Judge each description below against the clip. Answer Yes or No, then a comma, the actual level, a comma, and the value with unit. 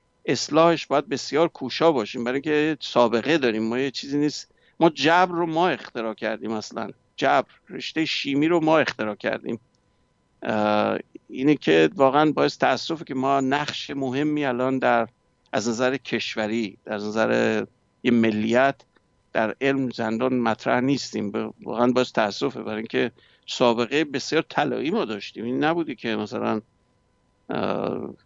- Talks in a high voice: No, low, 125 Hz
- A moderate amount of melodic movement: Yes, average, 4.9 semitones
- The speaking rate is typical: Yes, average, 135 wpm